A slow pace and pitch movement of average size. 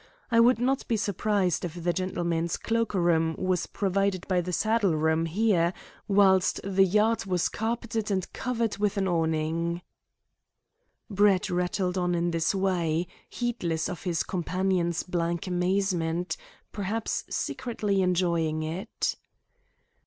Yes: slow, 130 wpm; average, 3.1 semitones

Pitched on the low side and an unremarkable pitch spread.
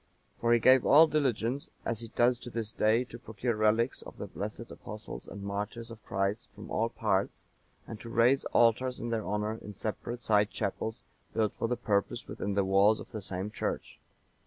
No: low, 110 Hz; narrow, 2.3 semitones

